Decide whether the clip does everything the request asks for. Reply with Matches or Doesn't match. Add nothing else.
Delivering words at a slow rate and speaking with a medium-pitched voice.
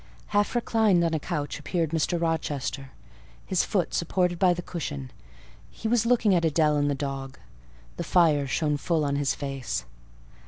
Doesn't match